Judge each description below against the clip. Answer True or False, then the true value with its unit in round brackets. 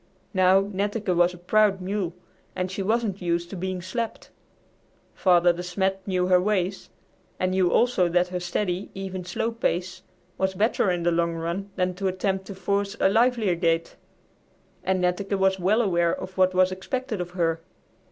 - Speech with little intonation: True (1.9 semitones)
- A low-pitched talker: False (185 Hz)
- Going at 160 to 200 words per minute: True (175 wpm)